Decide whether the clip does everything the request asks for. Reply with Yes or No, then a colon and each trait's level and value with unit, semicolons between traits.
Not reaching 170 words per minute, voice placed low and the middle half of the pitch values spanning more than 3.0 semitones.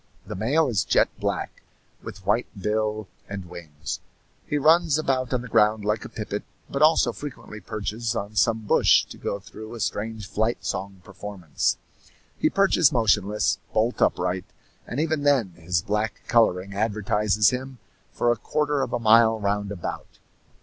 Yes: average, 160 wpm; low, 110 Hz; average, 3.5 semitones